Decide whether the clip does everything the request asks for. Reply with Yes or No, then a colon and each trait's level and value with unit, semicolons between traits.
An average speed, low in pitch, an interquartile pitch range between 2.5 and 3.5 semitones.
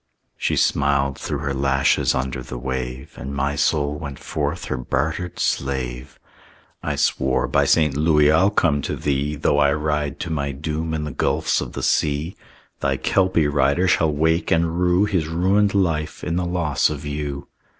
Yes: average, 175 wpm; very low, 75 Hz; average, 2.8 semitones